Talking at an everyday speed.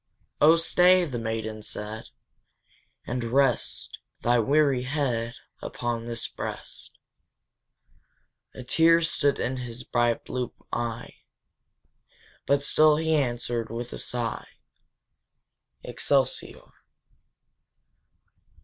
No: slow, 95 wpm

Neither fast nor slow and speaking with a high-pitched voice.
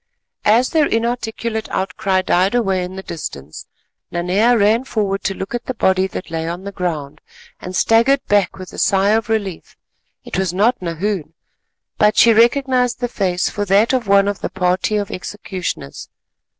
Yes: average, 175 wpm; high, 200 Hz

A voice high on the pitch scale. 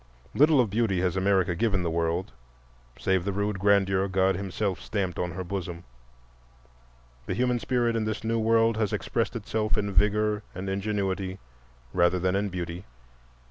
No: low, 100 Hz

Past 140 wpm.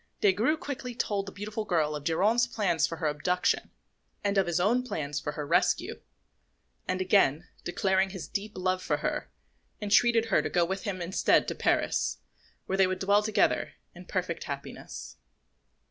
Yes: average, 175 wpm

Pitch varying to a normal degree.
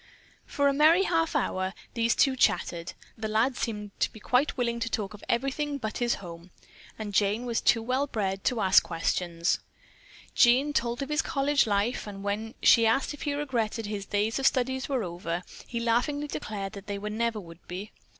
Yes: average, 4.6 semitones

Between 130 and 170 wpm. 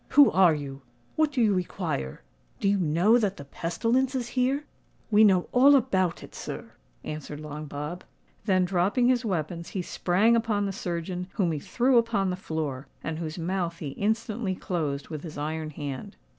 No: average, 180 wpm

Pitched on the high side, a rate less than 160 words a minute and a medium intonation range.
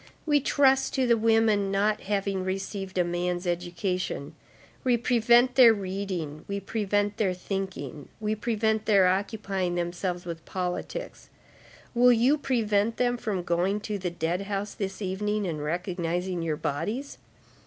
Yes: high, 195 Hz; average, 145 wpm; average, 3.6 semitones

